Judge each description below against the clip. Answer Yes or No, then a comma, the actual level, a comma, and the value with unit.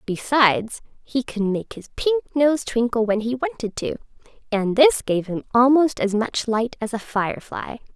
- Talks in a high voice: Yes, high, 240 Hz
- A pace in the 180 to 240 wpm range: No, average, 165 wpm